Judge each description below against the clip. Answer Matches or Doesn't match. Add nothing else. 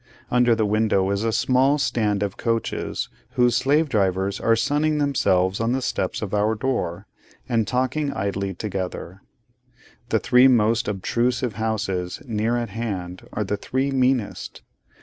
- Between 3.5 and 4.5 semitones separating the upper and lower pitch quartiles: Matches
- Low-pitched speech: Matches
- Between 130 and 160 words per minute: Matches